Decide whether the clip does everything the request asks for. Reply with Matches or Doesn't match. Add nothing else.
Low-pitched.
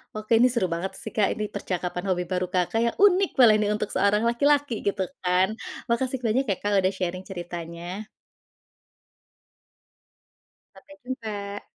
Doesn't match